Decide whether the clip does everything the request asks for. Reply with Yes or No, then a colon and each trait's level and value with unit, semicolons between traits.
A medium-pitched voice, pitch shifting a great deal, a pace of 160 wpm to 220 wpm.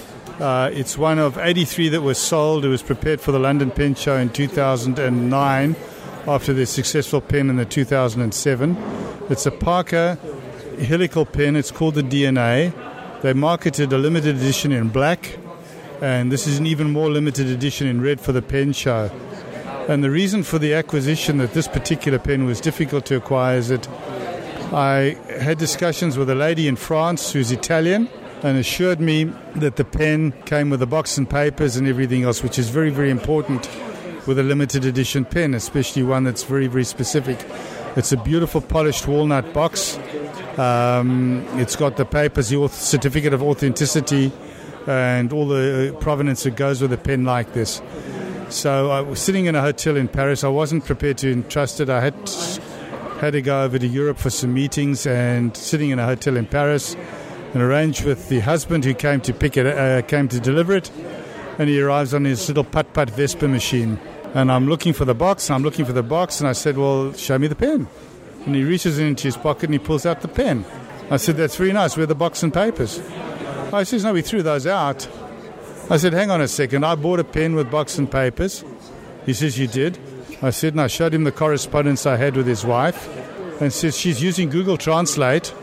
No: medium, 145 Hz; average, 3.0 semitones; average, 200 wpm